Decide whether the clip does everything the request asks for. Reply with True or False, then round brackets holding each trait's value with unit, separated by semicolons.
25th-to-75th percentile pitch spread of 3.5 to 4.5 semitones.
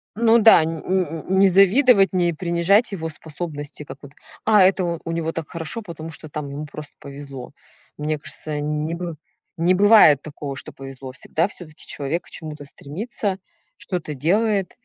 True (4.2 semitones)